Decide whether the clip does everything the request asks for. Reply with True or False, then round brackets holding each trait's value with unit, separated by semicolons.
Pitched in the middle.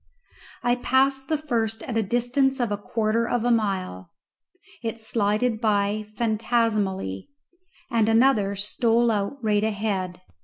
False (225 Hz)